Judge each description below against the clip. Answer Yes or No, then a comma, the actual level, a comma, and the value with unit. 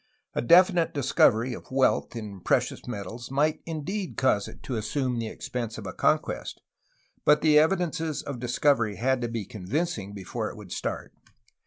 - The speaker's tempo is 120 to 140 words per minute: No, average, 165 wpm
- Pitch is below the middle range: Yes, low, 125 Hz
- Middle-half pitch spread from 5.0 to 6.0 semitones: Yes, wide, 5.5 semitones